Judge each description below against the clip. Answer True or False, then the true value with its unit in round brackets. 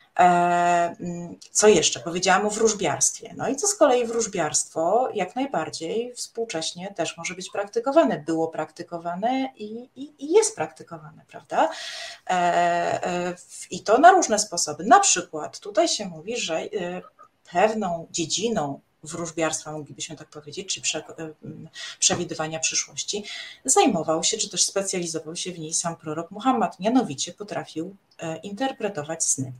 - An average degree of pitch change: False (5.7 semitones)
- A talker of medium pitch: True (175 Hz)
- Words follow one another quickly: False (125 wpm)